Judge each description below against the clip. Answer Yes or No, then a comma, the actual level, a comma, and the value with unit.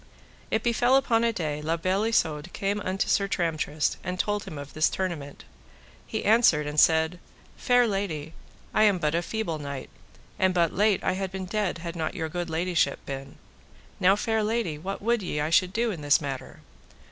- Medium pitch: Yes, medium, 180 Hz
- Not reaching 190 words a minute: No, average, 195 wpm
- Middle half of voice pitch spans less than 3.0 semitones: No, average, 4.9 semitones